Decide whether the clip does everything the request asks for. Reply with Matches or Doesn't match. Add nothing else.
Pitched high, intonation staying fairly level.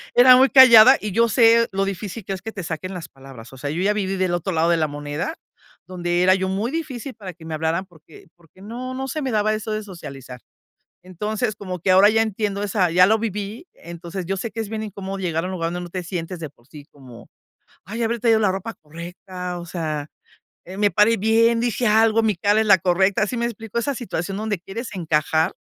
Doesn't match